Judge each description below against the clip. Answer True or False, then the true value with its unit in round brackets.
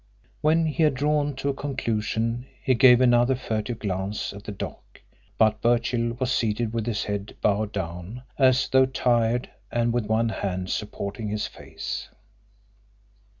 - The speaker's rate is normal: True (150 wpm)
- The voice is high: False (115 Hz)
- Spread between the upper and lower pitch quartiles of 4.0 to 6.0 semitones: False (3.5 semitones)